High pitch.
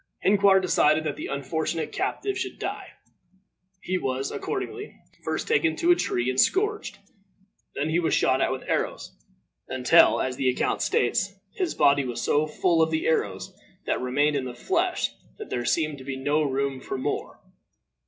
No: medium, 150 Hz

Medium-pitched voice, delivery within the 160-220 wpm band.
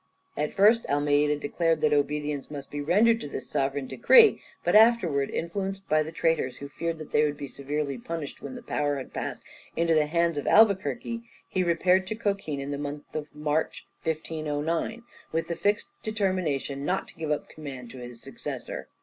Yes: medium, 155 Hz; average, 190 wpm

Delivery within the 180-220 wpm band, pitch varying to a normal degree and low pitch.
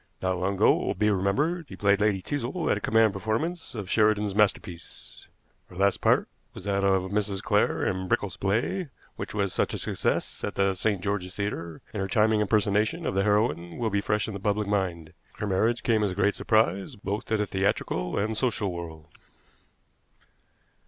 No: average, 195 wpm; narrow, 2.2 semitones; low, 100 Hz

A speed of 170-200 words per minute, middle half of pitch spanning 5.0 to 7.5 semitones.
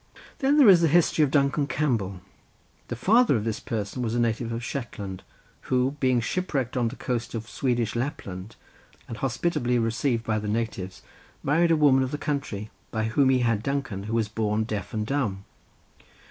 No: average, 185 wpm; average, 4.1 semitones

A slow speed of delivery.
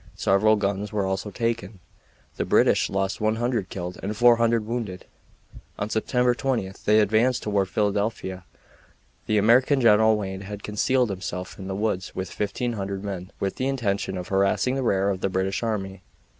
No: average, 160 wpm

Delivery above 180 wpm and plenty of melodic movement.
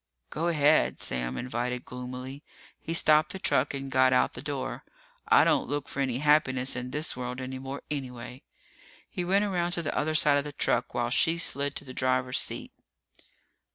No: average, 190 wpm; average, 3.0 semitones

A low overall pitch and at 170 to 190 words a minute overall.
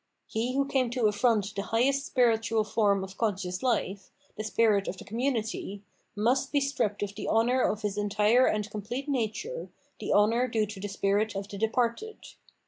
No: high, 220 Hz; average, 185 wpm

